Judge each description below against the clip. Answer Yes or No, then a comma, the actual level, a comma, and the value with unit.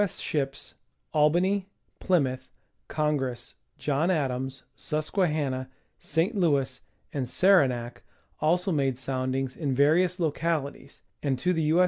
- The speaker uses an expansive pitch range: No, average, 4.4 semitones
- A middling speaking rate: No, slow, 110 wpm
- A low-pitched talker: No, medium, 150 Hz